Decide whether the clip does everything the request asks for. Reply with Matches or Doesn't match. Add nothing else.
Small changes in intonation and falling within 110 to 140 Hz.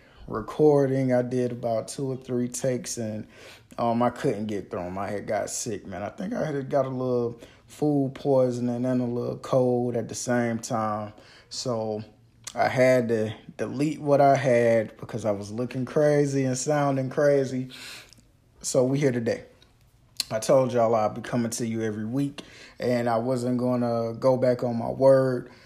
Matches